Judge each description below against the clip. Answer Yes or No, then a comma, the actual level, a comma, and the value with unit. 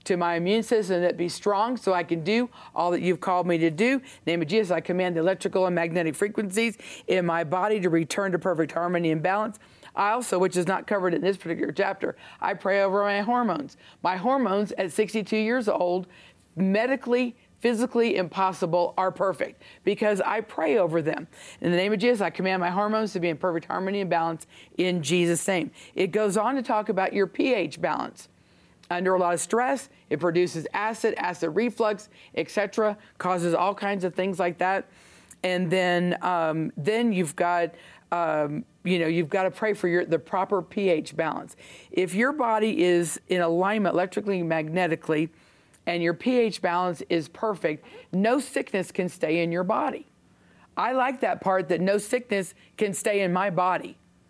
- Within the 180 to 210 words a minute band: Yes, average, 185 wpm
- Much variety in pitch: No, average, 3.3 semitones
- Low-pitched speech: No, medium, 185 Hz